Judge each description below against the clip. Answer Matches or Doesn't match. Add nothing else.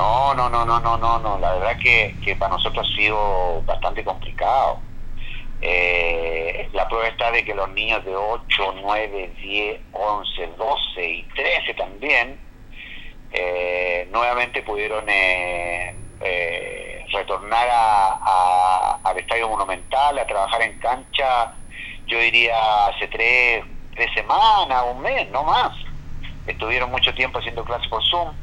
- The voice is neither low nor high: Doesn't match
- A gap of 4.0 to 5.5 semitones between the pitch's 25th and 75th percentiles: Matches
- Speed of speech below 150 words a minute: Matches